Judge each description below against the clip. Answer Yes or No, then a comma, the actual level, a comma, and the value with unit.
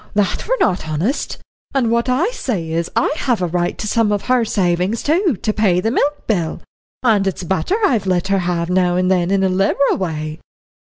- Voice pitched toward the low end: No, high, 195 Hz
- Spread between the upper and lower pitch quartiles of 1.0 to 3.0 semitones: No, average, 4.9 semitones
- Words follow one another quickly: Yes, fast, 210 wpm